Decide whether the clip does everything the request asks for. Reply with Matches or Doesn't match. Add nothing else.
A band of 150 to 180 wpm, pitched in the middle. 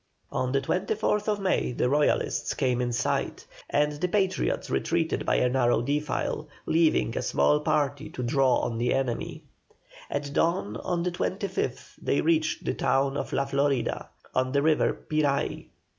Matches